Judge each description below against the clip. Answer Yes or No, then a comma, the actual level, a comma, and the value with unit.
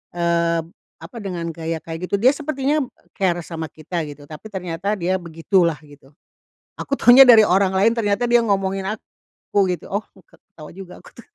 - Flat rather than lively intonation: No, average, 4.2 semitones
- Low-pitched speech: No, medium, 185 Hz